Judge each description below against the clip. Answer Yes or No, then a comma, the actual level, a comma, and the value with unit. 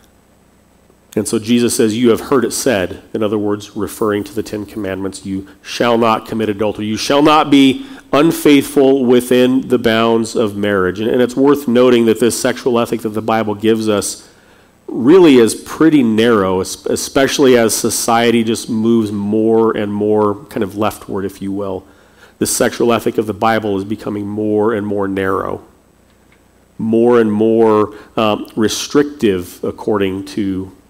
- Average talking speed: Yes, average, 160 wpm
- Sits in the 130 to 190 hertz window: No, low, 110 Hz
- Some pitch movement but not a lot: No, narrow, 2.3 semitones